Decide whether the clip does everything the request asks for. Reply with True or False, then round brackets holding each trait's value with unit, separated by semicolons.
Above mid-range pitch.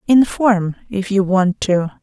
True (200 Hz)